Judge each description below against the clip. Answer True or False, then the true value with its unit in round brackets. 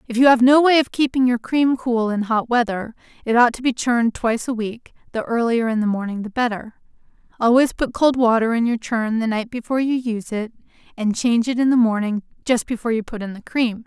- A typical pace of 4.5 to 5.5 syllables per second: False (5.8 syllables/s)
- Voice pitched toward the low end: False (235 Hz)